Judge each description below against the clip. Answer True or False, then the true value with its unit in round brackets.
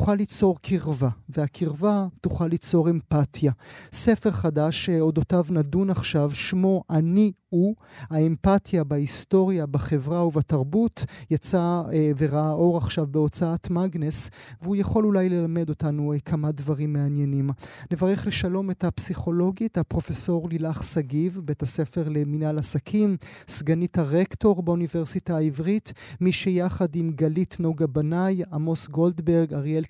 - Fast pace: False (115 wpm)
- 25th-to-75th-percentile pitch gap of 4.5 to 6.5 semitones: False (3.3 semitones)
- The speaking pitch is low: False (165 Hz)